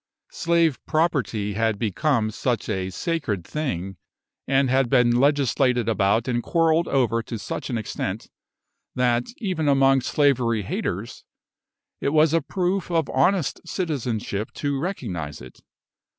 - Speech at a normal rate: No, slow, 130 wpm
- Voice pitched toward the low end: Yes, low, 130 Hz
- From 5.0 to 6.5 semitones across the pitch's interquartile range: Yes, wide, 5.6 semitones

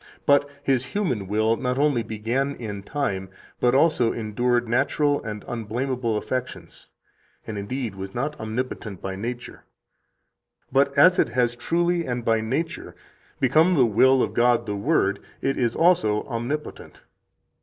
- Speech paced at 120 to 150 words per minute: Yes, average, 145 wpm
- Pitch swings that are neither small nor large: Yes, average, 4.0 semitones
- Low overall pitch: Yes, low, 120 Hz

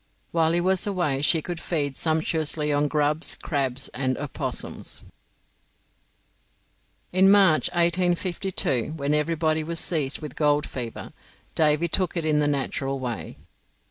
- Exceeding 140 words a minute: No, slow, 135 wpm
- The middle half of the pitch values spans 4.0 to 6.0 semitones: No, average, 3.0 semitones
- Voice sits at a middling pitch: Yes, medium, 155 Hz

